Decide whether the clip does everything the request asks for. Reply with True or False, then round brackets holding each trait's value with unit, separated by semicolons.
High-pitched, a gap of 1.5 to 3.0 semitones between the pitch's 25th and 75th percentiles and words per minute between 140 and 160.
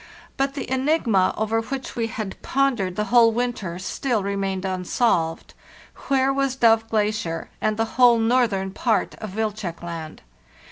False (220 Hz; 4.3 semitones; 150 wpm)